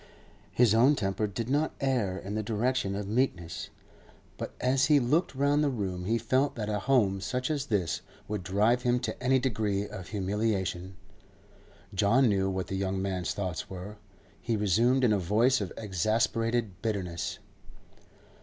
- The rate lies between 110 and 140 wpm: No, average, 165 wpm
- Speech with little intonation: No, average, 4.5 semitones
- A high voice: No, low, 110 Hz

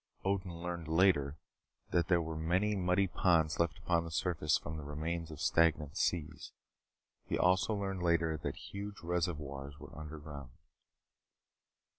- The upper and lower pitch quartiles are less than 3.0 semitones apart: Yes, narrow, 2.6 semitones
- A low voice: Yes, very low, 85 Hz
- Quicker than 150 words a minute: No, average, 140 wpm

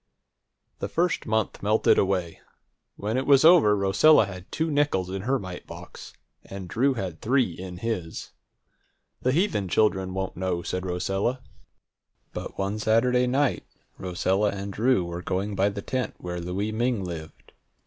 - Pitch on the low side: Yes, low, 100 Hz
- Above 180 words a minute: No, average, 155 wpm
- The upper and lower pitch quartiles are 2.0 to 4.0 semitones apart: No, average, 5.1 semitones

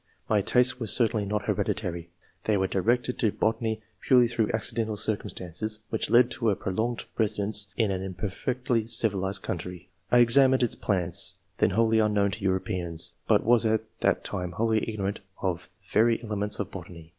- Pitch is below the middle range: Yes, low, 105 Hz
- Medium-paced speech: Yes, average, 170 wpm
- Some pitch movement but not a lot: Yes, average, 3.1 semitones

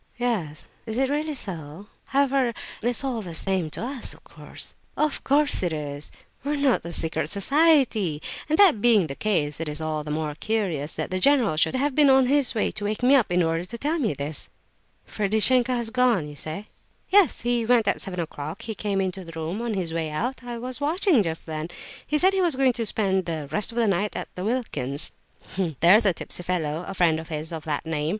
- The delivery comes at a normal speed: No, fast, 220 wpm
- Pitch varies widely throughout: Yes, wide, 7.8 semitones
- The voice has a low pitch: No, high, 205 Hz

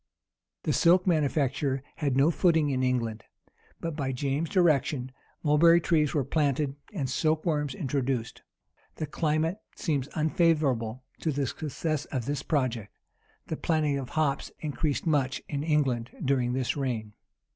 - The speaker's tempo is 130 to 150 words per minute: Yes, average, 140 wpm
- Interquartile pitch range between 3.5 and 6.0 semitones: No, average, 3.1 semitones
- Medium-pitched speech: Yes, medium, 145 Hz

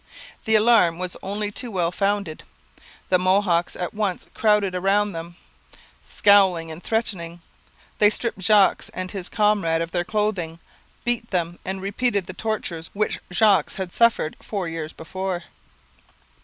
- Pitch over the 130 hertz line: Yes, high, 190 Hz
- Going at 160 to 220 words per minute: No, average, 140 wpm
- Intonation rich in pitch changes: No, average, 3.2 semitones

